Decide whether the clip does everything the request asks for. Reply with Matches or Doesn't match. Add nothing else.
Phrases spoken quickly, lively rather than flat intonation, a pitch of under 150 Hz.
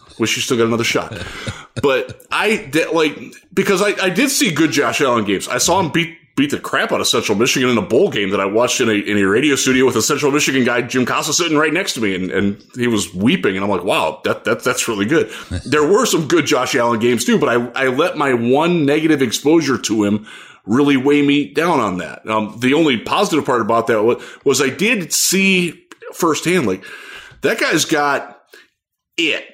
Matches